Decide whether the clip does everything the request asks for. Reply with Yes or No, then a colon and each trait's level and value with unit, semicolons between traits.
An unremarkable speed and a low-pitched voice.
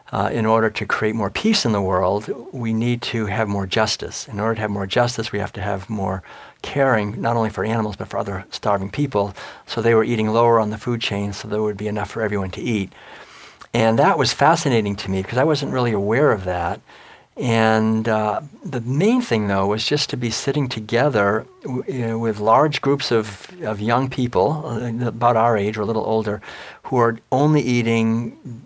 No: fast, 215 wpm; low, 115 Hz